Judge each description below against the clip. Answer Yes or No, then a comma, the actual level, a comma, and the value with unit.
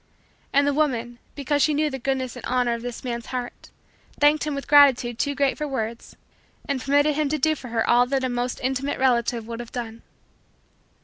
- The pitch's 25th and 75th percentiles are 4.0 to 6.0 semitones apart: No, average, 3.0 semitones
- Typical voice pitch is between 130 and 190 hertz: No, very high, 260 Hz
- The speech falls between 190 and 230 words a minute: Yes, fast, 205 wpm